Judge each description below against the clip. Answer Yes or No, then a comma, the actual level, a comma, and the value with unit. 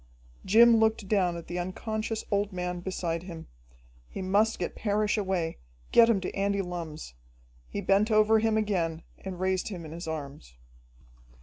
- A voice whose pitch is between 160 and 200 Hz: Yes, high, 190 Hz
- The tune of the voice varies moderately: Yes, average, 3.6 semitones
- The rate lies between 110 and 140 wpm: No, average, 165 wpm